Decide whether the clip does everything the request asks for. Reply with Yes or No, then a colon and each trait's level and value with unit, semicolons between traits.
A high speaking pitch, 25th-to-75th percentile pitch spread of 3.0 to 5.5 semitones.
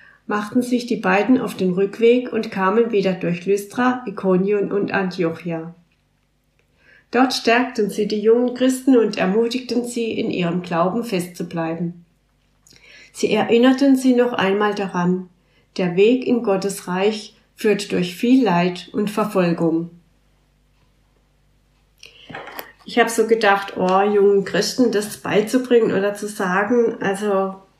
Yes: high, 205 Hz; average, 3.8 semitones